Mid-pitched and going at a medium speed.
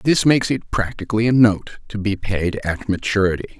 No: low, 105 Hz; average, 185 wpm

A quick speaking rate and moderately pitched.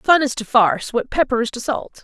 No: fast, 265 wpm; high, 240 Hz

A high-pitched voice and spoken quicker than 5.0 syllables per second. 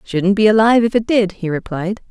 Yes: high, 205 Hz; 5.6 syllables/s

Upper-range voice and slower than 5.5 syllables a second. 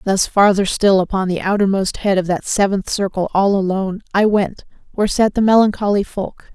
Yes: high, 195 Hz; 5.3 syllables/s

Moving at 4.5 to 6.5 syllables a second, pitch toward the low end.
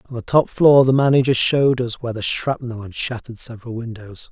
Yes: 5.7 syllables/s; low, 120 Hz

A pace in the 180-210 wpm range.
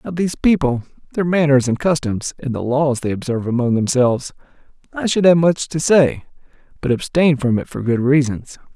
Yes: average, 185 wpm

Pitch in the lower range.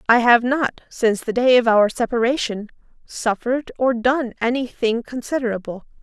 No: high, 240 Hz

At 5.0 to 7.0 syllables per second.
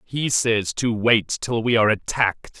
No: 4.6 syllables/s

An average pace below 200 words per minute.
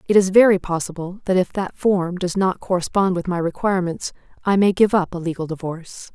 No: fast, 205 wpm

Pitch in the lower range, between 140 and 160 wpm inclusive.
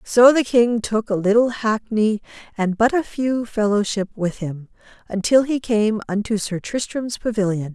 No: high, 220 Hz; average, 155 wpm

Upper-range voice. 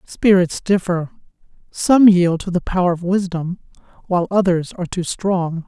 No: medium, 180 Hz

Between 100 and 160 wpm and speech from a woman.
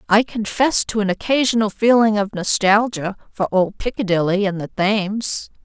Yes: average, 150 wpm; female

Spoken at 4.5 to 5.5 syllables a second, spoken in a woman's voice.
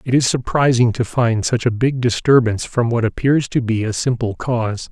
No: 5.2 syllables/s; male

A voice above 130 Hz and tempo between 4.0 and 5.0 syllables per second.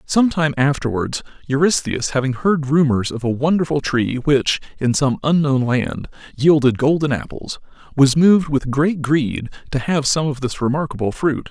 Yes: medium, 140 Hz; 4.9 syllables/s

